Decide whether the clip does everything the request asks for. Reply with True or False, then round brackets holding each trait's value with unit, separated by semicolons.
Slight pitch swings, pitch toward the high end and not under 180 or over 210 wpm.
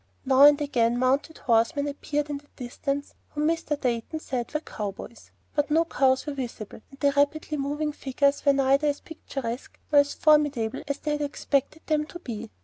True (2.3 semitones; 285 Hz; 190 wpm)